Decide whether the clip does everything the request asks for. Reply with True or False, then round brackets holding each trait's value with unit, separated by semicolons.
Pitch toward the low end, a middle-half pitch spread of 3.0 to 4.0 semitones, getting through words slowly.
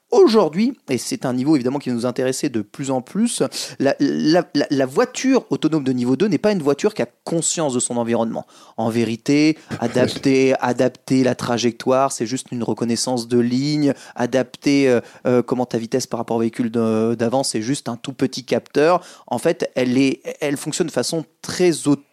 False (130 Hz; 3.6 semitones; 190 wpm)